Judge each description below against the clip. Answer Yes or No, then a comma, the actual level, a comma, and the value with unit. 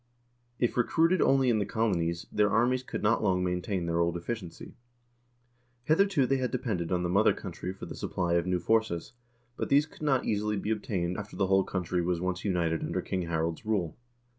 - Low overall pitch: Yes, very low, 95 Hz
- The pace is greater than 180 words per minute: Yes, average, 195 wpm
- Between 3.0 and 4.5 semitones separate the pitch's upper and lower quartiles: No, average, 5.1 semitones